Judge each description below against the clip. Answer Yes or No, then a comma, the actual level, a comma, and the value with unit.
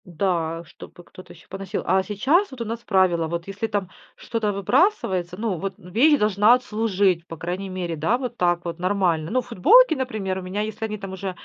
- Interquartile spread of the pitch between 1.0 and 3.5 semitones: No, average, 3.9 semitones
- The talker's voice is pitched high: Yes, high, 195 Hz